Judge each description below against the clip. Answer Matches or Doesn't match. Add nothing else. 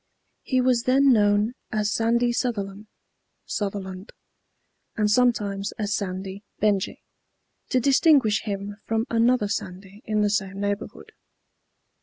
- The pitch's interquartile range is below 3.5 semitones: Matches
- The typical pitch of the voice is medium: Doesn't match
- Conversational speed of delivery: Doesn't match